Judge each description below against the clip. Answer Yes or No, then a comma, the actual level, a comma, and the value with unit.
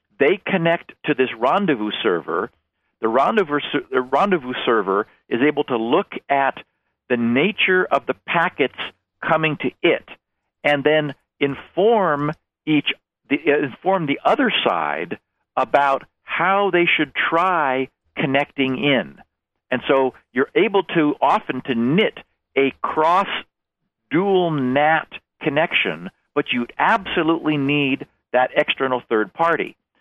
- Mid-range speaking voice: Yes, medium, 145 Hz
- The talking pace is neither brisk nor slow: No, slow, 120 wpm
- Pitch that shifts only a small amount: No, average, 4.2 semitones